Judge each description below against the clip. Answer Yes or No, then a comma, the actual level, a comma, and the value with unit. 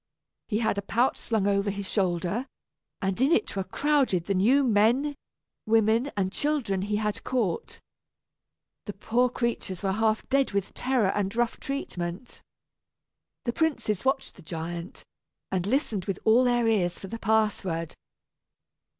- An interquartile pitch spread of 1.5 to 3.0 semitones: No, average, 4.3 semitones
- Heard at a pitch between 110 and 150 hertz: No, high, 215 Hz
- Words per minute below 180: Yes, average, 150 wpm